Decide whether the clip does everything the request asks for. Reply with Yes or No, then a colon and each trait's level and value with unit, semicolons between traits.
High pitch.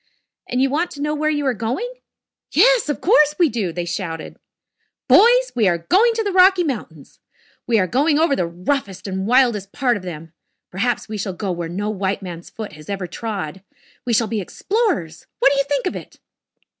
Yes: high, 230 Hz